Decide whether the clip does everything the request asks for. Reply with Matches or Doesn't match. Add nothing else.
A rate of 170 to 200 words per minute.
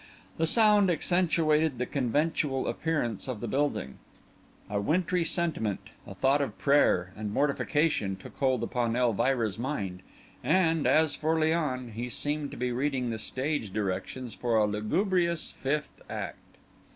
Doesn't match